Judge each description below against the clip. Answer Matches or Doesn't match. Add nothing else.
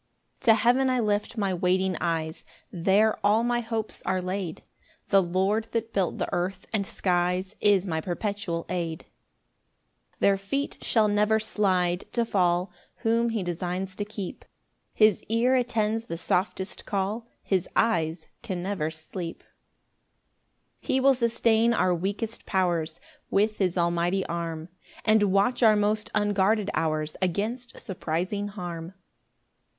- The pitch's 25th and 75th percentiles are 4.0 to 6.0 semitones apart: Doesn't match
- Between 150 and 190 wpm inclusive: Doesn't match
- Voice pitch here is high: Matches